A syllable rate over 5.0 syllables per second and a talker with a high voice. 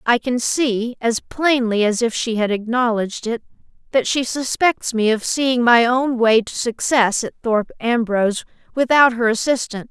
No: 4.6 syllables/s; high, 235 Hz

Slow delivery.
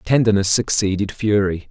Yes: slow, 105 wpm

